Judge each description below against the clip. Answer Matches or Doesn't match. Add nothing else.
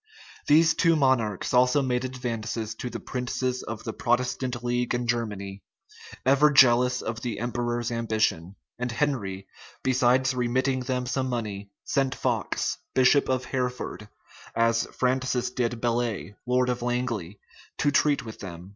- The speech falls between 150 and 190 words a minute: Doesn't match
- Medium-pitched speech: Doesn't match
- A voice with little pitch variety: Matches